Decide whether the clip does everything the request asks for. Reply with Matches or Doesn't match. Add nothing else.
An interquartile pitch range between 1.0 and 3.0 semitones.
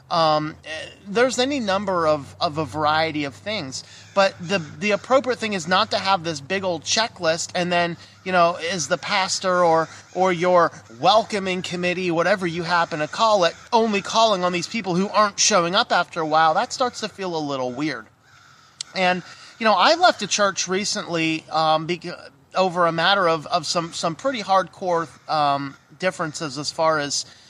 Doesn't match